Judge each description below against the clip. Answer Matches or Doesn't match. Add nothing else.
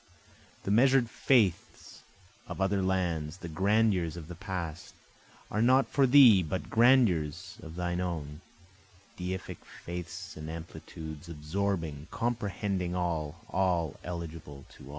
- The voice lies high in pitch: Doesn't match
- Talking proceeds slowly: Matches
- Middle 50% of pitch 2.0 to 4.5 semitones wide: Matches